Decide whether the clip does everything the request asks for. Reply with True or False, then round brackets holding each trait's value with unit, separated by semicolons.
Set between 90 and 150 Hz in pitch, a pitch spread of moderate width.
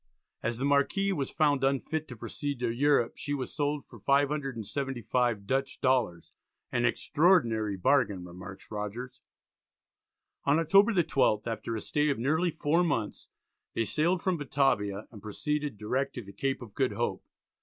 True (135 Hz; 4.6 semitones)